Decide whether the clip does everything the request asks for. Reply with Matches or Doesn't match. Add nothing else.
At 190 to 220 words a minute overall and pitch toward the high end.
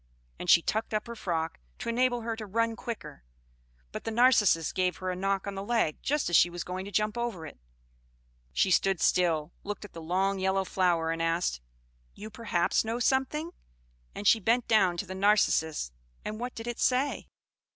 Matches